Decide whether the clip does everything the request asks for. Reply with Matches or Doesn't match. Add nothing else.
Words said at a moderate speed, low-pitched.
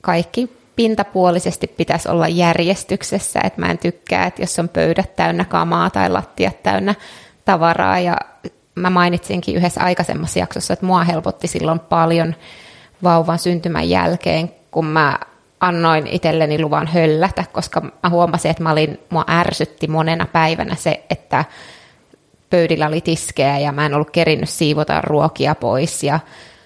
Doesn't match